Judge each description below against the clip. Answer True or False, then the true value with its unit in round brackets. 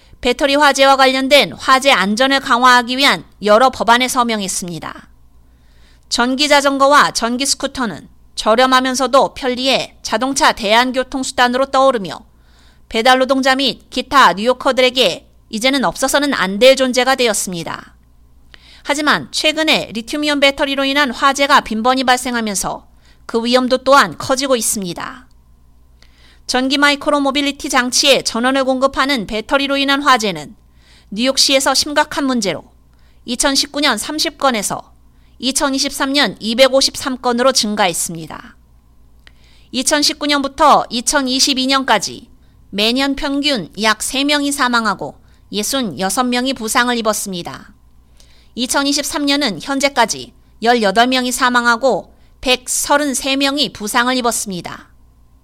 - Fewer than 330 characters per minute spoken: True (260 characters per minute)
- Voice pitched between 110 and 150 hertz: False (255 Hz)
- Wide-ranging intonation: False (4.8 semitones)